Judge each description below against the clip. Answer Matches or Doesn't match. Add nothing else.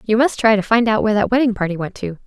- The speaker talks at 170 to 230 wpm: Doesn't match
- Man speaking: Doesn't match